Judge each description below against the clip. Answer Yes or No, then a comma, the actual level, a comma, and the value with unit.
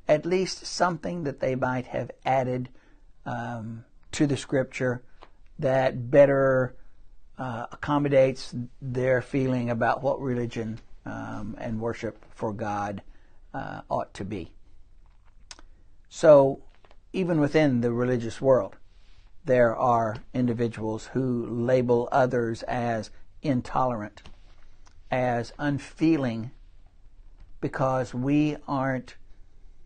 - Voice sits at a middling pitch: No, low, 120 Hz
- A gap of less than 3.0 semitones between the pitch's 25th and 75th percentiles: No, average, 4.1 semitones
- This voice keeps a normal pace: No, slow, 100 wpm